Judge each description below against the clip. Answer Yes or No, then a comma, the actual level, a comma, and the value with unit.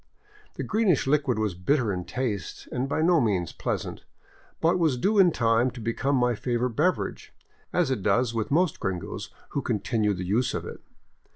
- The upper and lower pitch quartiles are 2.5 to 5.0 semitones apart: No, wide, 5.5 semitones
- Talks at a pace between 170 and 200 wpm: Yes, average, 185 wpm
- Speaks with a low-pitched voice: Yes, low, 125 Hz